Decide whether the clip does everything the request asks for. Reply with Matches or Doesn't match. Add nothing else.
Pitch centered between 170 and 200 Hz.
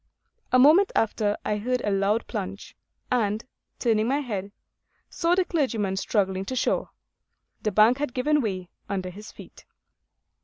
Doesn't match